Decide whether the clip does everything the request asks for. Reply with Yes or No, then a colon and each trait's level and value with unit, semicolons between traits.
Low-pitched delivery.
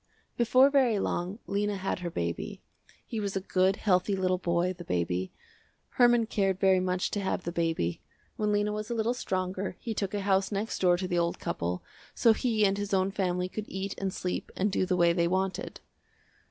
No: high, 190 Hz